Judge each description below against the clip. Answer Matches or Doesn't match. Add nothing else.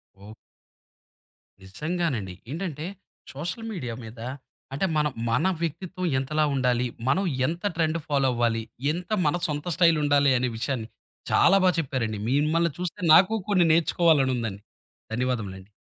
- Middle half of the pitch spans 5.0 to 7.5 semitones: Matches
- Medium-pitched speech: Matches